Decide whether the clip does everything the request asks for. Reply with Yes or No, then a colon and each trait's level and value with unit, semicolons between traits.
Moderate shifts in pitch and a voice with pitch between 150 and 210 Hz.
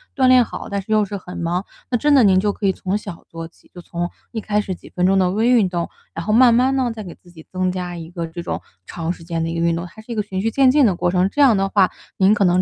Yes: average, 3.7 semitones; high, 190 Hz